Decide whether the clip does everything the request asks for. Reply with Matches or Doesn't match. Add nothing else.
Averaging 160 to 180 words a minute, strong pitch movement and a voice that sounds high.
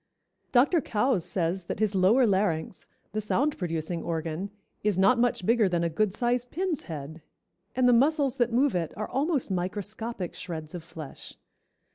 Matches